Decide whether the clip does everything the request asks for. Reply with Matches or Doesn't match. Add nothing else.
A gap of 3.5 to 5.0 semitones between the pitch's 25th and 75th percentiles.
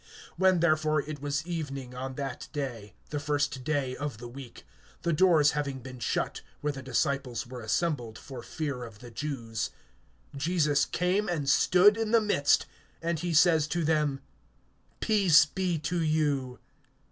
Matches